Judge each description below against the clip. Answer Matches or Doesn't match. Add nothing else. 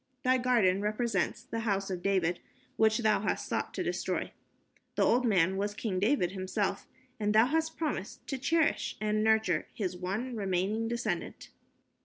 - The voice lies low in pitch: Doesn't match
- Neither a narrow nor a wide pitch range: Matches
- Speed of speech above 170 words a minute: Doesn't match